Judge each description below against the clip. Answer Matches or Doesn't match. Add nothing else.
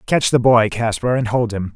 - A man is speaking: Matches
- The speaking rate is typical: Doesn't match